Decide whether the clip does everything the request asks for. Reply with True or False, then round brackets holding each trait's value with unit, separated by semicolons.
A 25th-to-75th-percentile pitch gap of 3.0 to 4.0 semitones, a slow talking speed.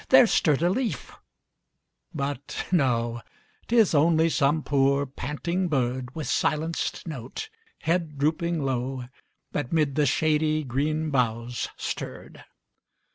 True (3.5 semitones; 115 wpm)